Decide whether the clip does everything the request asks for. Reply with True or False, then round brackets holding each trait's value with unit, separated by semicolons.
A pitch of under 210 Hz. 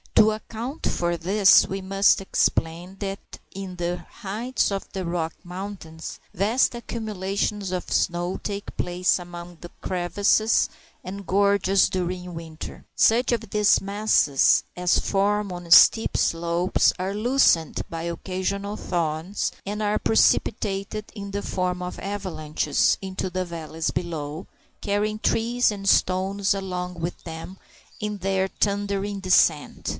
True (190 Hz)